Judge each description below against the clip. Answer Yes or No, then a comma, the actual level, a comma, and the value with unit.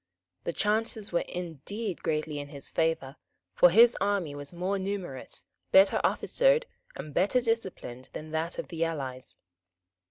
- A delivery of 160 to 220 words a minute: No, average, 145 wpm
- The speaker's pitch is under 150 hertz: No, medium, 175 Hz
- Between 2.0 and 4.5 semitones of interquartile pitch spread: No, average, 5.1 semitones